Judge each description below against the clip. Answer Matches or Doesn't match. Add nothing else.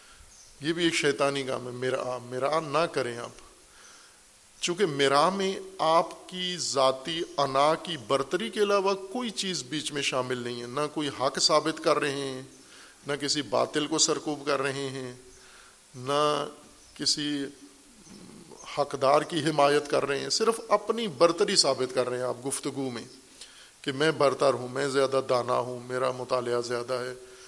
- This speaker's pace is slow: Doesn't match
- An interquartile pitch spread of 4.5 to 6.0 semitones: Doesn't match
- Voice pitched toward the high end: Doesn't match